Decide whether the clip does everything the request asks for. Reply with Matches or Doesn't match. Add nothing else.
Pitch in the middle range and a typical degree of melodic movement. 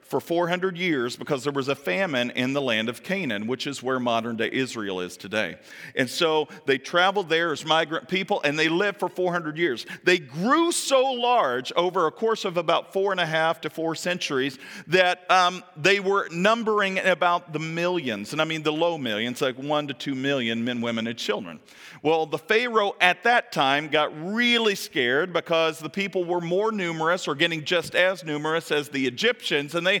Matches